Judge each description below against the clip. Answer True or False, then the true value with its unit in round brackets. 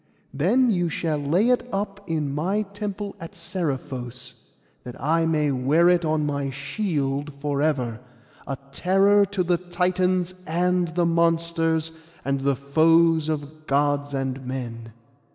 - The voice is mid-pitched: True (160 Hz)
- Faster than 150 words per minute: False (140 wpm)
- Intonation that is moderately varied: True (4.3 semitones)